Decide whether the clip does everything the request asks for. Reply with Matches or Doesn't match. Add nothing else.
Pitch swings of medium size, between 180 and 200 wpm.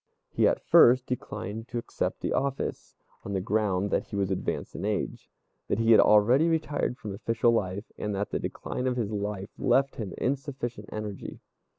Matches